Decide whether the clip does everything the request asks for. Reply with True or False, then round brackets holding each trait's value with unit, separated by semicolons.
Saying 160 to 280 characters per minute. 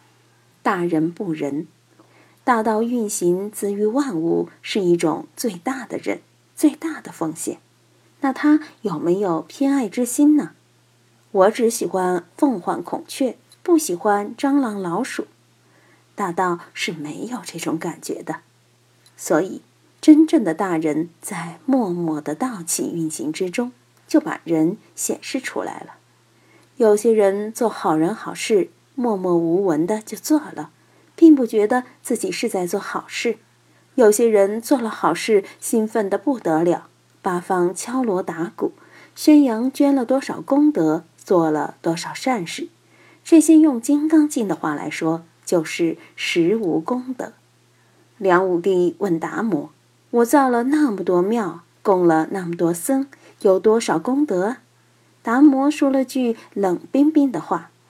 True (200 characters per minute)